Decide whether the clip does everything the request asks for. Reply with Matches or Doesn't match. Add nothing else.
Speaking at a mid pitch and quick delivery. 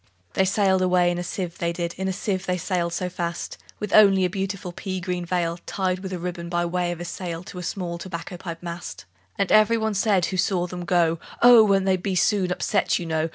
Matches